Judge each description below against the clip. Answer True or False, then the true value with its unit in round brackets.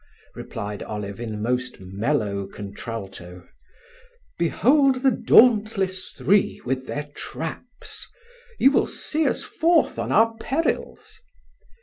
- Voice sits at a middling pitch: True (145 Hz)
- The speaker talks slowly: True (105 wpm)